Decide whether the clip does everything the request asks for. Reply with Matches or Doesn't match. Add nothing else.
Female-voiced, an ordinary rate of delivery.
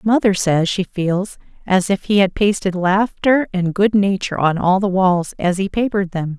Matches